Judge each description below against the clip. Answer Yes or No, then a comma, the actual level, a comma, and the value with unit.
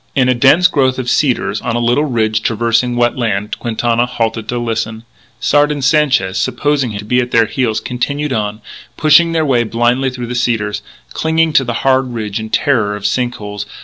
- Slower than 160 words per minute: No, average, 200 wpm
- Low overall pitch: Yes, low, 120 Hz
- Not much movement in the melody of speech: No, average, 3.3 semitones